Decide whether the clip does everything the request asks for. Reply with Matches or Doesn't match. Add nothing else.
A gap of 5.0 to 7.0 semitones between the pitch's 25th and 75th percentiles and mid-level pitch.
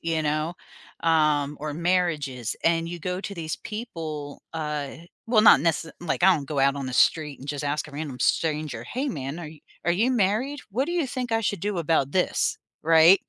Doesn't match